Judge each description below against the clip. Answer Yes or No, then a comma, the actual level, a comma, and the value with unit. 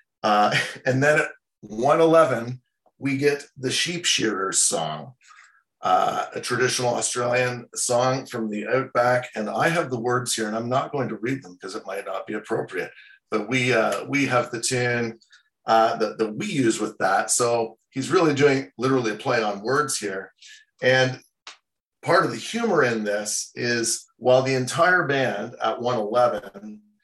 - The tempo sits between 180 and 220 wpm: No, average, 170 wpm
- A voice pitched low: Yes, low, 125 Hz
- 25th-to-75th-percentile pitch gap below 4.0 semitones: Yes, average, 3.3 semitones